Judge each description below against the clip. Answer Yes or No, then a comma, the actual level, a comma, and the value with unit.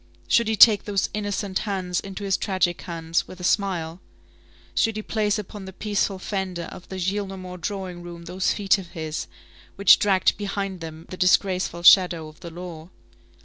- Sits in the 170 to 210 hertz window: Yes, medium, 185 Hz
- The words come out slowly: No, average, 175 wpm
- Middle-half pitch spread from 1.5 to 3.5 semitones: Yes, narrow, 2.5 semitones